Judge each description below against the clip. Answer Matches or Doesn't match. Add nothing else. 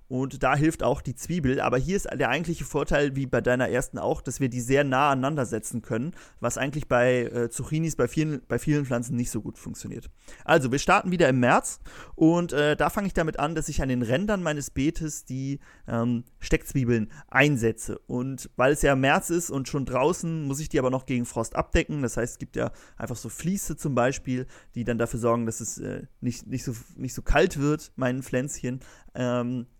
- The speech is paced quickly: Matches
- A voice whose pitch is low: Matches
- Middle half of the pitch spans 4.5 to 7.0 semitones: Doesn't match